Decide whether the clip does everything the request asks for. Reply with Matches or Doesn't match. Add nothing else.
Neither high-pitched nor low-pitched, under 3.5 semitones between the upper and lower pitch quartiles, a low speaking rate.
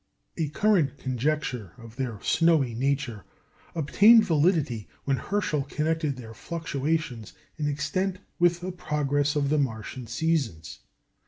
Doesn't match